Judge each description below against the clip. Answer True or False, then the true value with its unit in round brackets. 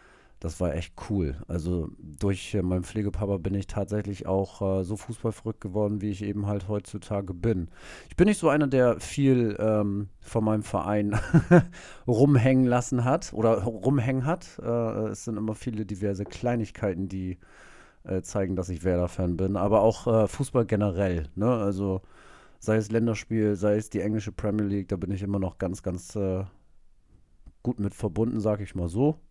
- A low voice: True (105 Hz)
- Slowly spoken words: False (170 wpm)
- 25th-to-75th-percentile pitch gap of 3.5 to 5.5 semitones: False (2.9 semitones)